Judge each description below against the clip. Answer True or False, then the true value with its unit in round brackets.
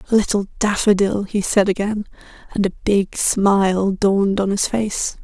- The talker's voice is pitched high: True (200 Hz)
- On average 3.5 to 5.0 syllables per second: True (4.5 syllables/s)